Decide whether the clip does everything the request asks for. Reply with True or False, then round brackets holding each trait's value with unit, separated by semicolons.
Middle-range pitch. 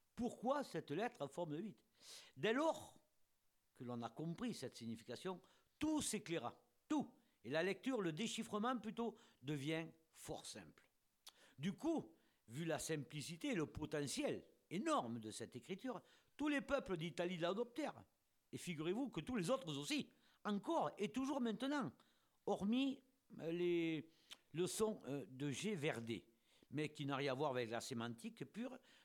True (170 Hz)